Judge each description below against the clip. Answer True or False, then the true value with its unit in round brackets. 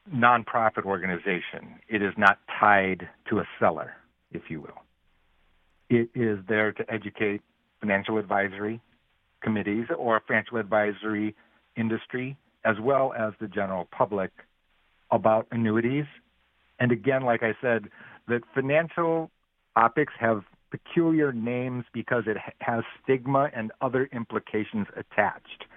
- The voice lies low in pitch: True (115 Hz)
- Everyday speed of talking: False (120 wpm)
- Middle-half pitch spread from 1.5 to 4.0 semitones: True (2.8 semitones)